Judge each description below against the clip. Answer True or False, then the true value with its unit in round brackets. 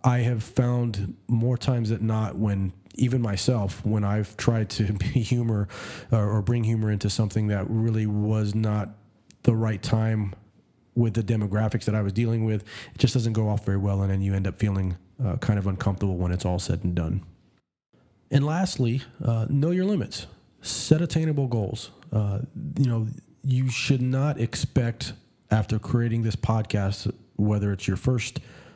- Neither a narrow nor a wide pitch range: True (3.2 semitones)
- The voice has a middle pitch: False (110 Hz)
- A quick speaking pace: False (175 wpm)